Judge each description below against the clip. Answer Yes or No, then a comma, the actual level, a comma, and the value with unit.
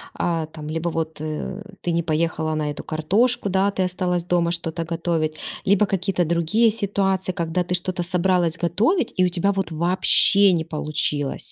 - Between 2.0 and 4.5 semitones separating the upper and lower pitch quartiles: Yes, average, 2.8 semitones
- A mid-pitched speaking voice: Yes, medium, 175 Hz